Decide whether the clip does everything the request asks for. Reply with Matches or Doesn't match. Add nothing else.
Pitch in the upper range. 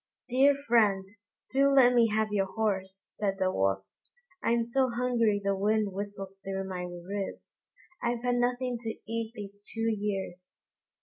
Matches